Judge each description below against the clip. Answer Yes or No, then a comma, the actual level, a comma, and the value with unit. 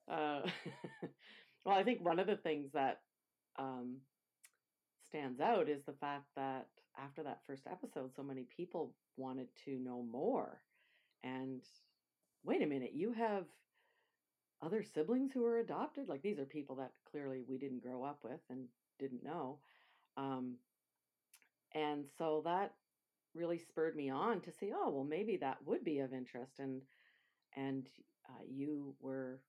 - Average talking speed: Yes, average, 155 wpm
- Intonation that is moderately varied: Yes, average, 4.6 semitones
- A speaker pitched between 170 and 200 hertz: No, medium, 140 Hz